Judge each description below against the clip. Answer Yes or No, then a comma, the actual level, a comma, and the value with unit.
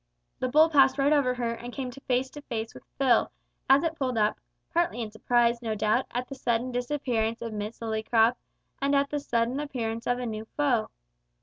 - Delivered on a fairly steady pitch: No, average, 3.2 semitones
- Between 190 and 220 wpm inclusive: Yes, average, 200 wpm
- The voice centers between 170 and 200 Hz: No, high, 245 Hz